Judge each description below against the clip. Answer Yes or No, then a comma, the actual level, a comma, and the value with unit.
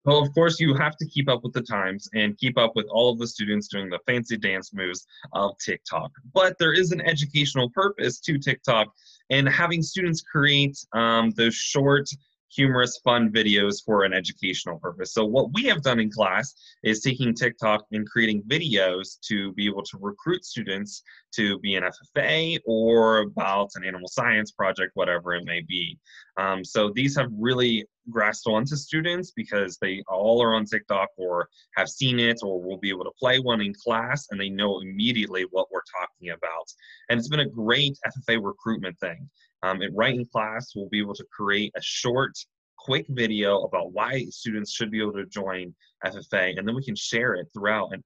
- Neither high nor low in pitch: No, low, 115 Hz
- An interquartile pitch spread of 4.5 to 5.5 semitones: Yes, average, 5.2 semitones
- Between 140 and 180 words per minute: No, average, 190 wpm